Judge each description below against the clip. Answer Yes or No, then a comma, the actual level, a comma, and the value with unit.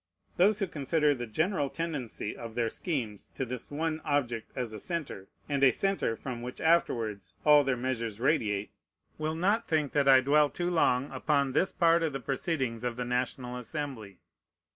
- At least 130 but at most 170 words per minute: No, average, 180 wpm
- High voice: No, low, 135 Hz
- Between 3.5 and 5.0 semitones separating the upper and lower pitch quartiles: Yes, average, 4.7 semitones